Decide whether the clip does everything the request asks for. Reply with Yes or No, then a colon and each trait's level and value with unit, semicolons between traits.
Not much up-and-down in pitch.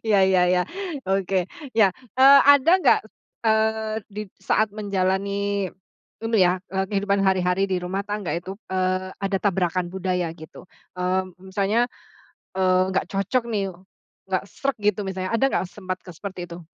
Yes: narrow, 2.0 semitones